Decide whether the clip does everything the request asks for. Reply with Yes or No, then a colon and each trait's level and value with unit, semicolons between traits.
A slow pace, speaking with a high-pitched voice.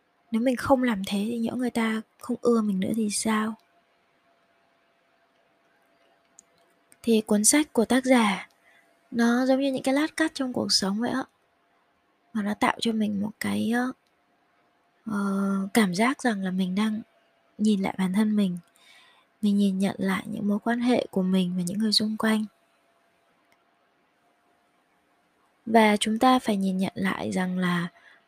Yes: slow, 160 wpm; high, 220 Hz